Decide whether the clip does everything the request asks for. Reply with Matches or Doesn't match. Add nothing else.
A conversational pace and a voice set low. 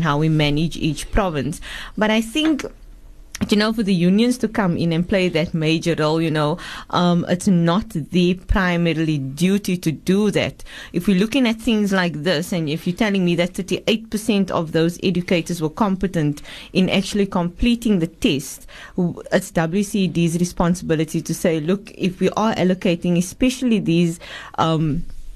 Doesn't match